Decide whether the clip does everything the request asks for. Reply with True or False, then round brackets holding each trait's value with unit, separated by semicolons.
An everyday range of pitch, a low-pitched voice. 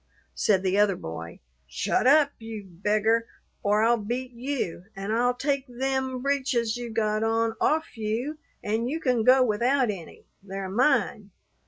False (3.7 semitones; 230 Hz)